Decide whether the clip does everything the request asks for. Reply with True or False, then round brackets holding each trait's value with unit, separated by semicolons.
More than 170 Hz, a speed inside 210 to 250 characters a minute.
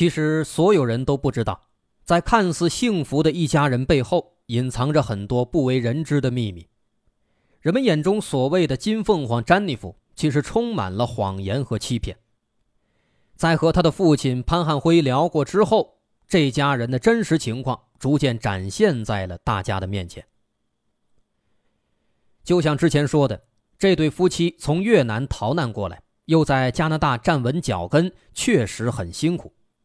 False (140 Hz; 235 characters per minute)